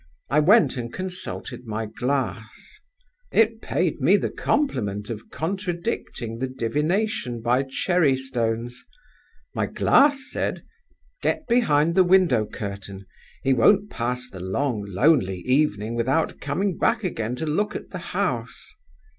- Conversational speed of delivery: No, slow, 130 wpm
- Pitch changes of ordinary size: No, wide, 7.8 semitones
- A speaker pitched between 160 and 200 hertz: No, low, 135 Hz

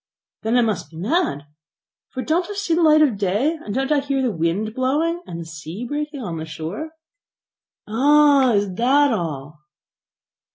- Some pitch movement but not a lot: No, wide, 8.5 semitones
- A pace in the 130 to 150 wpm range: No, average, 175 wpm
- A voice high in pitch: Yes, high, 245 Hz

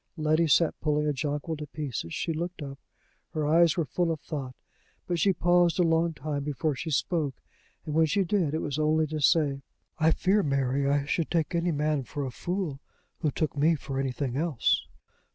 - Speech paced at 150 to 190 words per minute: No, average, 200 wpm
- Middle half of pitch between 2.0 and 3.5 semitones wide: Yes, average, 2.9 semitones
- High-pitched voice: No, medium, 155 Hz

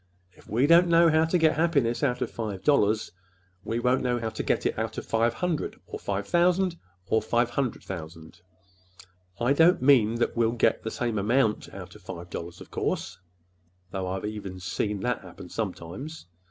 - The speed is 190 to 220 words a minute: Yes, average, 195 wpm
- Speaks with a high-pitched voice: No, low, 110 Hz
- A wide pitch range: Yes, wide, 6.9 semitones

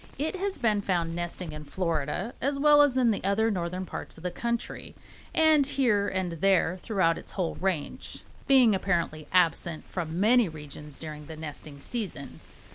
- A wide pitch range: Yes, wide, 6.3 semitones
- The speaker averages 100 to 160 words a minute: No, average, 170 wpm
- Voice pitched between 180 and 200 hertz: Yes, medium, 185 Hz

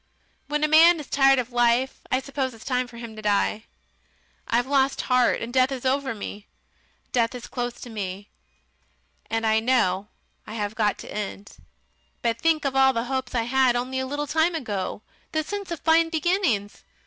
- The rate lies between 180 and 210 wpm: Yes, average, 195 wpm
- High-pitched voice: Yes, very high, 255 Hz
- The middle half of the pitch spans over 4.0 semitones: No, average, 3.7 semitones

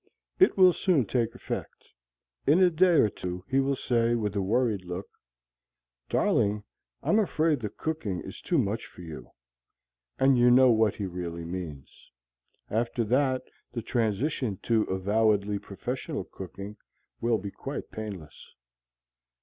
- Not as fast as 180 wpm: Yes, average, 140 wpm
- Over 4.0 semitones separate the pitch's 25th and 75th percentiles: Yes, average, 5.0 semitones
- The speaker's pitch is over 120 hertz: No, low, 110 Hz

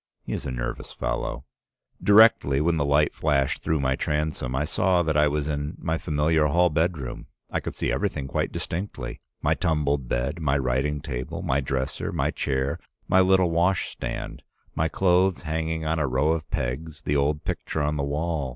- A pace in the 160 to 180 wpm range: No, average, 190 wpm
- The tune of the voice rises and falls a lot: No, average, 3.0 semitones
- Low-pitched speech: Yes, very low, 75 Hz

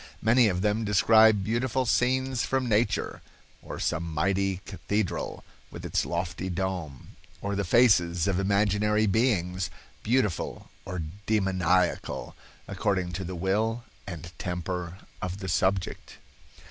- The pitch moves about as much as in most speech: Yes, average, 3.3 semitones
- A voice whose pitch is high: No, very low, 95 Hz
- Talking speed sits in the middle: No, slow, 120 wpm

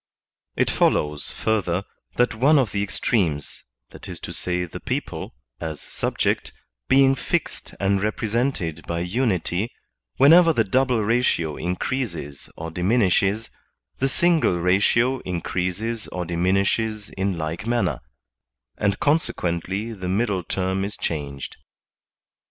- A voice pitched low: Yes, low, 100 Hz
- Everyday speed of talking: No, slow, 115 wpm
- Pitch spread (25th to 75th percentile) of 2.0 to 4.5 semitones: No, average, 5.0 semitones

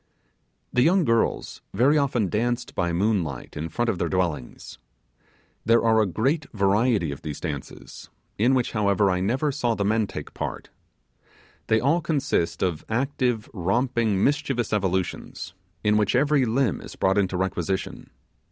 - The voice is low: Yes, low, 110 Hz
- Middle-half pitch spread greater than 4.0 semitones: Yes, average, 5.1 semitones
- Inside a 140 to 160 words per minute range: Yes, average, 150 wpm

